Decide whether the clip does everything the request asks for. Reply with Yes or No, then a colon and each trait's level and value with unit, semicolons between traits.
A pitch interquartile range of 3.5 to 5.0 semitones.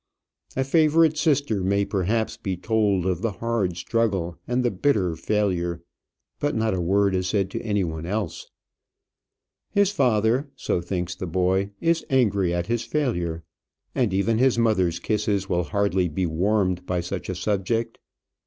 Yes: average, 4.3 semitones